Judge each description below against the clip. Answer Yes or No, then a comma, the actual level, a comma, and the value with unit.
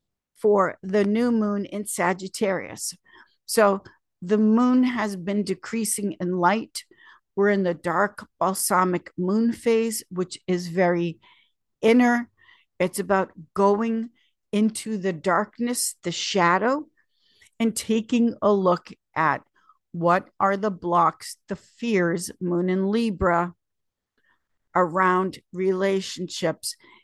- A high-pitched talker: Yes, high, 200 Hz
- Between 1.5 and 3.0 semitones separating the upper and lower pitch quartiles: No, average, 3.8 semitones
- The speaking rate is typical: No, slow, 110 wpm